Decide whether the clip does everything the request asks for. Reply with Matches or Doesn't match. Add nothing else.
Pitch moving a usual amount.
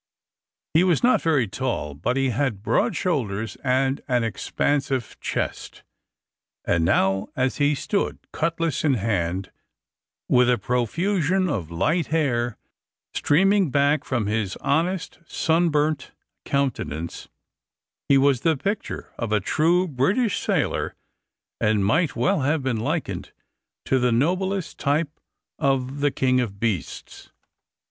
Doesn't match